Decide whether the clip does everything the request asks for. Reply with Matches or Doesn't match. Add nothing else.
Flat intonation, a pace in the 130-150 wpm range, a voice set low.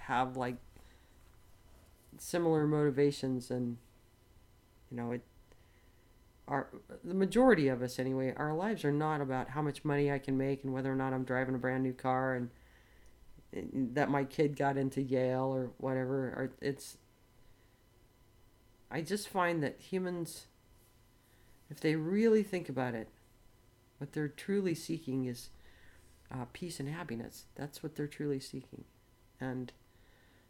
Doesn't match